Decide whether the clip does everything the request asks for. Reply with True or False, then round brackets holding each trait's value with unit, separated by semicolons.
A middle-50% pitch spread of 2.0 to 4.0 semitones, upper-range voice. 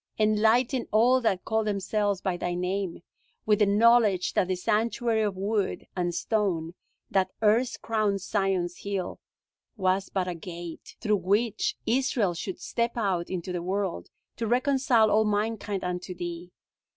True (3.3 semitones; 200 Hz)